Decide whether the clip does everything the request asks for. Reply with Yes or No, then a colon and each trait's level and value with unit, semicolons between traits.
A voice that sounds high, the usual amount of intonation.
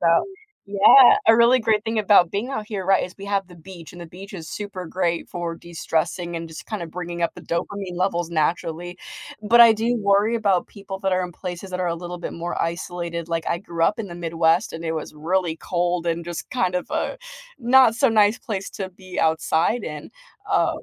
No: medium, 180 Hz; average, 3.3 semitones